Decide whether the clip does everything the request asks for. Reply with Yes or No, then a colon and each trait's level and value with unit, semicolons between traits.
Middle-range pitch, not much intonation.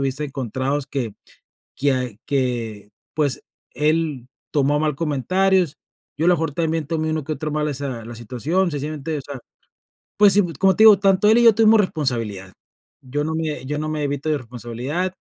No: medium, 150 Hz; average, 3.8 semitones